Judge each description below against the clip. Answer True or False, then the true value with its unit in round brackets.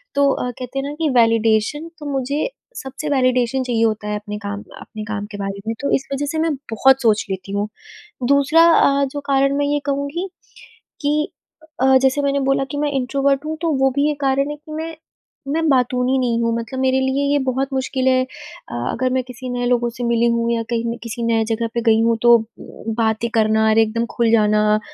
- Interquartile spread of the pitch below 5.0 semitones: True (3.5 semitones)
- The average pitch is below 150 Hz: False (255 Hz)